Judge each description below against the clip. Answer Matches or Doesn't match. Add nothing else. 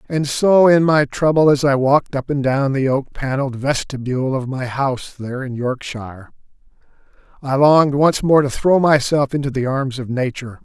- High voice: Doesn't match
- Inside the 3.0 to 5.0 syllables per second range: Doesn't match